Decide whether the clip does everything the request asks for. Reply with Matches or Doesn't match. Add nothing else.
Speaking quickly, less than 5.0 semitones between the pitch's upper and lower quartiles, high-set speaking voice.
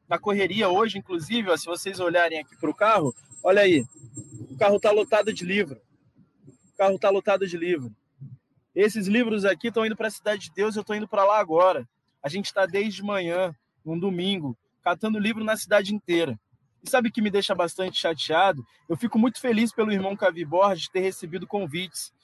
Matches